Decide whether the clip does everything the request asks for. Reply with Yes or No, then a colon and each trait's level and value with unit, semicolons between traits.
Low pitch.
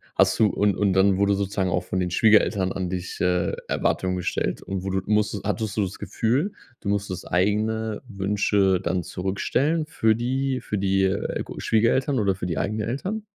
Yes: low, 100 Hz